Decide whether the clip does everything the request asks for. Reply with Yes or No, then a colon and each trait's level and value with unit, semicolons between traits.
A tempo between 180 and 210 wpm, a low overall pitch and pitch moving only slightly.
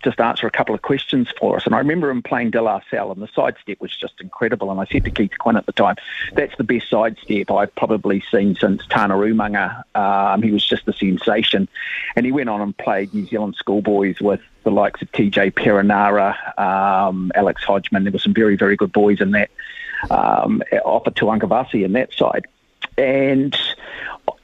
Yes: average, 200 wpm; low, 105 Hz; narrow, 1.9 semitones